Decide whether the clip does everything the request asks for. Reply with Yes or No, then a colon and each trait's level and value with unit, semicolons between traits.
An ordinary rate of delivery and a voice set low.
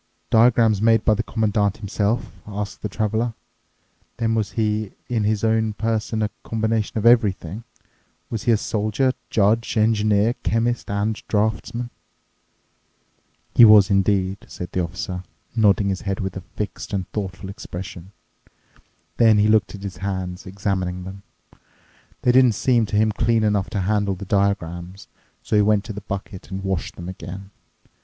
Yes: average, 155 wpm; low, 105 Hz